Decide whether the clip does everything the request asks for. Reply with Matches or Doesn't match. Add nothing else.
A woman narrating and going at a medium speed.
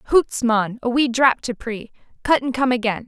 Doesn't match